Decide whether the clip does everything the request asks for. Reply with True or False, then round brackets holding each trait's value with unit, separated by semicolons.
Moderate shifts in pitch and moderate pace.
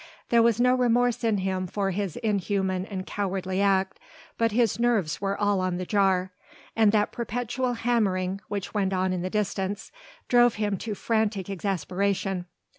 True (3.1 semitones; 165 wpm)